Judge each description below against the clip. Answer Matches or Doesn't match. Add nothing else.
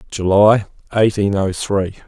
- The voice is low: Matches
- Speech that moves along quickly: Doesn't match